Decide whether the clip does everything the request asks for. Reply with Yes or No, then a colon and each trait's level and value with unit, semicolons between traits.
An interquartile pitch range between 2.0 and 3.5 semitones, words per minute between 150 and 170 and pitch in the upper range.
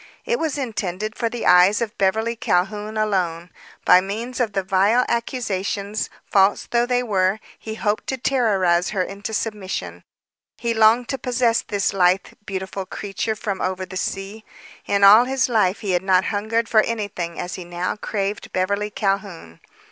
Yes: average, 3.2 semitones; average, 165 wpm; high, 205 Hz